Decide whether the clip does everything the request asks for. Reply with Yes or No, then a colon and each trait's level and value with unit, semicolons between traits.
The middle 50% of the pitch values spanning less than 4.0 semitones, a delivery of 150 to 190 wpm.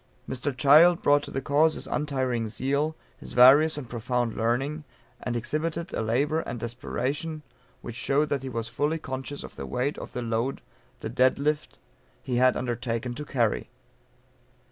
Yes: average, 3.6 semitones; average, 165 wpm